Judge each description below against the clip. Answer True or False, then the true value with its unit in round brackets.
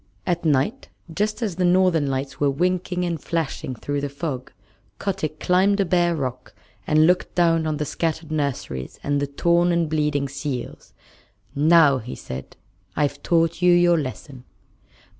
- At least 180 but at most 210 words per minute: False (160 wpm)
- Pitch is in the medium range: True (155 Hz)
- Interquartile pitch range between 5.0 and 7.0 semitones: False (3.7 semitones)